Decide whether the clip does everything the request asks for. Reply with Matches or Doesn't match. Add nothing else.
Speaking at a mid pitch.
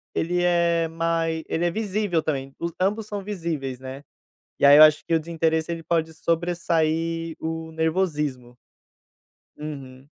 Matches